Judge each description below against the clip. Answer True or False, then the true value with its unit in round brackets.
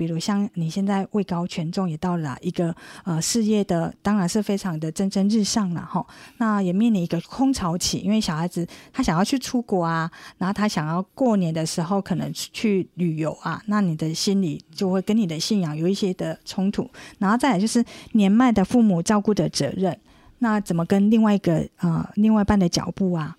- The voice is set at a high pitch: True (195 Hz)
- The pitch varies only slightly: False (3.7 semitones)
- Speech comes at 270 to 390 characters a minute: True (305 characters per minute)